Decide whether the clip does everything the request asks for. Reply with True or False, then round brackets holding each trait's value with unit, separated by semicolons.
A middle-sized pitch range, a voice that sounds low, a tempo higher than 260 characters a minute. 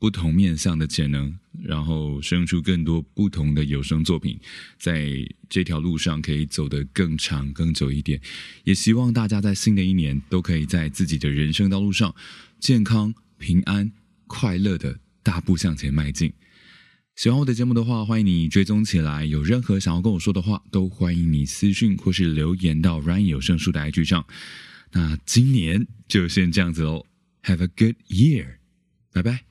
True (4.5 semitones; 90 Hz; 285 characters per minute)